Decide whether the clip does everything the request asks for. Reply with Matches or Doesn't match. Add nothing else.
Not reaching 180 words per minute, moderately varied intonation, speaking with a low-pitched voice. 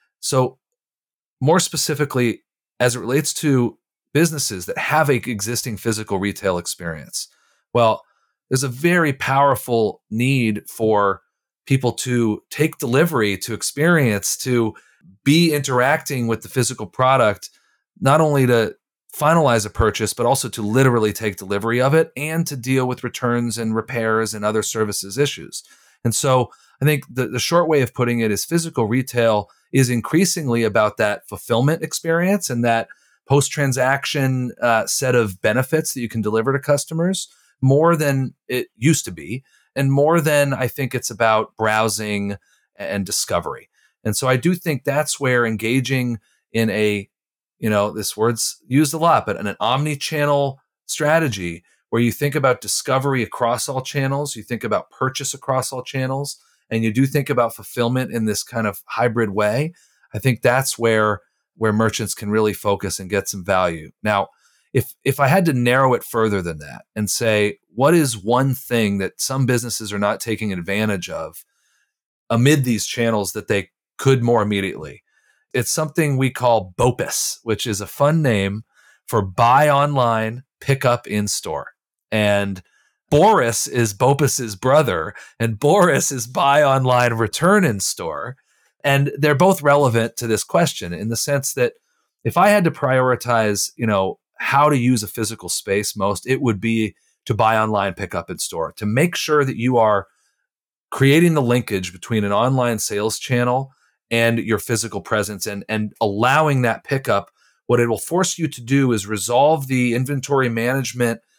Matches